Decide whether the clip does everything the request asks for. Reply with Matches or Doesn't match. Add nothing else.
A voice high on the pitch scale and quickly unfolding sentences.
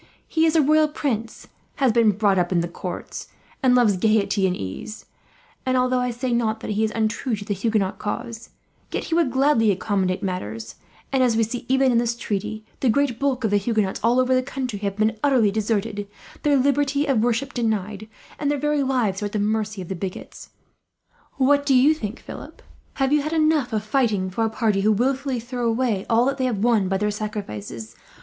Matches